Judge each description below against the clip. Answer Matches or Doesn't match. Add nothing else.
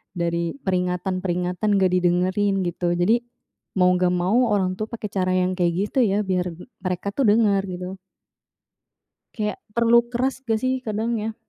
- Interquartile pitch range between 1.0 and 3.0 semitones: Doesn't match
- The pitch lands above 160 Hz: Matches